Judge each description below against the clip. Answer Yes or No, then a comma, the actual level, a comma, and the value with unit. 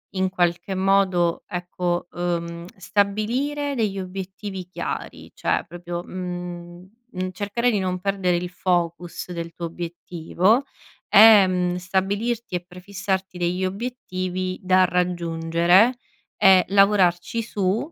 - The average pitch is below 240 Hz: Yes, medium, 185 Hz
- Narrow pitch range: Yes, narrow, 2.1 semitones